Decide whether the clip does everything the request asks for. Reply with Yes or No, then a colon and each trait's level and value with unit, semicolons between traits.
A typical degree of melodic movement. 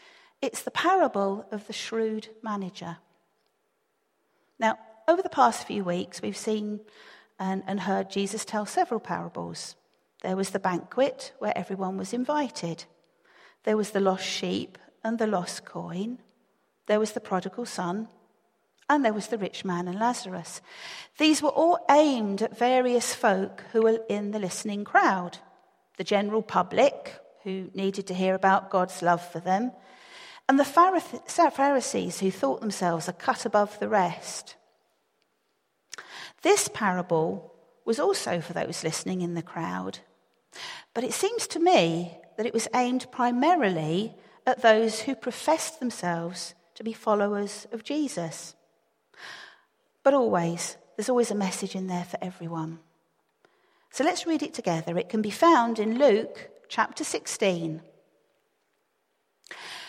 No: wide, 5.9 semitones